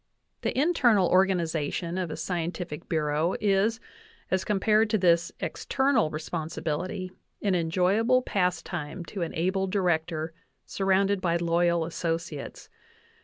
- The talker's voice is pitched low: No, medium, 180 Hz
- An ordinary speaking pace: No, slow, 120 wpm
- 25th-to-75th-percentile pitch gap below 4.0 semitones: Yes, average, 2.9 semitones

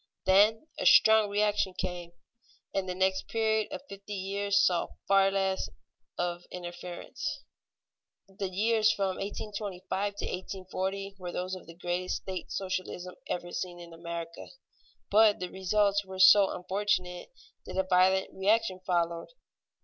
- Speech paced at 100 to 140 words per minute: Yes, slow, 135 wpm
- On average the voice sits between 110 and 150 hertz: No, high, 190 Hz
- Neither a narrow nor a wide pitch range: No, narrow, 1.9 semitones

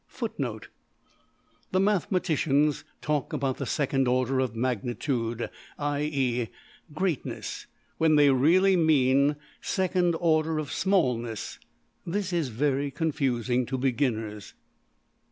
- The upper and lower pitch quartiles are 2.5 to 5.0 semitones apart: Yes, average, 4.2 semitones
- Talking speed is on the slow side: Yes, slow, 100 wpm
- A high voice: No, medium, 140 Hz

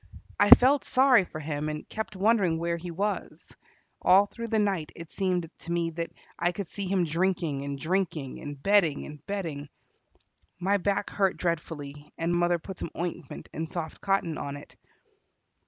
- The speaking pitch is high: No, medium, 175 Hz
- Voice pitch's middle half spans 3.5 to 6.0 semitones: Yes, average, 3.9 semitones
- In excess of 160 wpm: Yes, average, 170 wpm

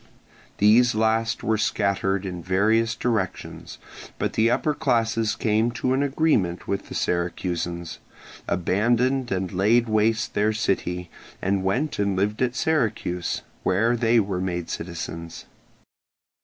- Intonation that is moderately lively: Yes, average, 3.9 semitones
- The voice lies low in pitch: Yes, low, 105 Hz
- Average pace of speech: No, slow, 130 wpm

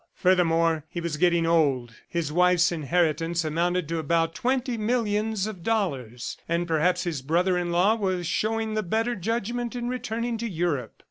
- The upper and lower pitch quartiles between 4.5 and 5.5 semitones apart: Yes, average, 4.9 semitones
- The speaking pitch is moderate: Yes, medium, 175 Hz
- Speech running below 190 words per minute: Yes, average, 160 wpm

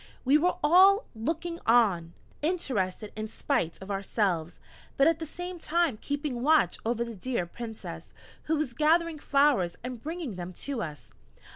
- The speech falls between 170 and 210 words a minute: No, average, 155 wpm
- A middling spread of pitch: No, wide, 7.3 semitones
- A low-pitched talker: No, very high, 255 Hz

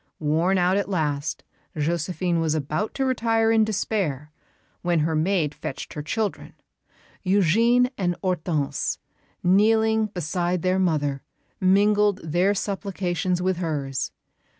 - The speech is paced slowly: Yes, slow, 120 wpm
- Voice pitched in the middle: Yes, medium, 180 Hz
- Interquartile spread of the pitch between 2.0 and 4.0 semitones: No, average, 4.4 semitones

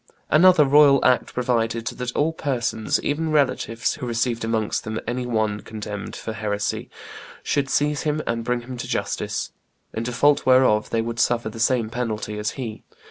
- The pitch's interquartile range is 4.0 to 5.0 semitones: No, average, 3.2 semitones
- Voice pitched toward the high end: No, low, 120 Hz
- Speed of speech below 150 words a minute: No, average, 170 wpm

